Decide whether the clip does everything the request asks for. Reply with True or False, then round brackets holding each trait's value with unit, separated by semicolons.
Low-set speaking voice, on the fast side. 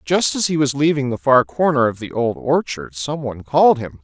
True (130 Hz; 240 wpm)